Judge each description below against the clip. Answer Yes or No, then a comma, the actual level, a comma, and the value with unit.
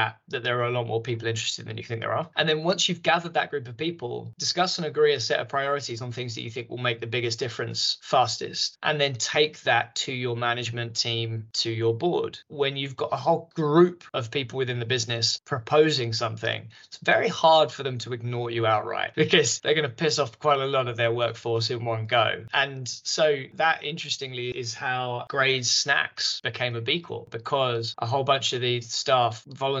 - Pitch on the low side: Yes, low, 125 Hz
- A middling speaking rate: No, fast, 215 wpm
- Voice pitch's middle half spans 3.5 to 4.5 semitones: Yes, average, 3.9 semitones